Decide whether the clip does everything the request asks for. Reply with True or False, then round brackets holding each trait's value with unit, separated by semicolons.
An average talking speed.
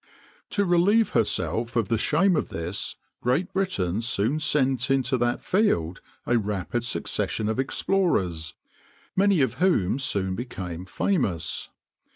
False (130 wpm)